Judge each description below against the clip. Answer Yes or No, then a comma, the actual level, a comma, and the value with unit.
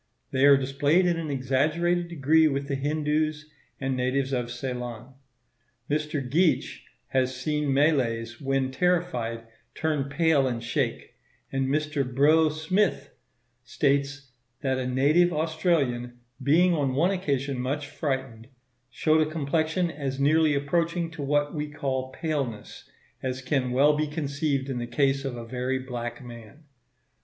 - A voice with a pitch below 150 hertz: Yes, medium, 140 Hz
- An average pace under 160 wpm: Yes, average, 140 wpm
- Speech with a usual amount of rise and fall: Yes, average, 3.0 semitones